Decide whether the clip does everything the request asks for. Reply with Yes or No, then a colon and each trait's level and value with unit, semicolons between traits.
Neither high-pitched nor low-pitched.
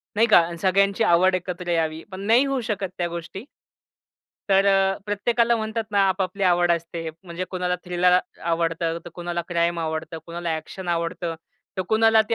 Yes: medium, 180 Hz